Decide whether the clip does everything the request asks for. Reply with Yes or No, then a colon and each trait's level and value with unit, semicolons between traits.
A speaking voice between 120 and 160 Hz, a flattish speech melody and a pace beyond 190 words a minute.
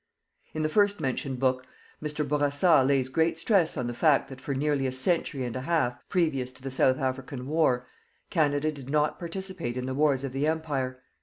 No: medium, 140 Hz; average, 3.2 semitones; average, 200 wpm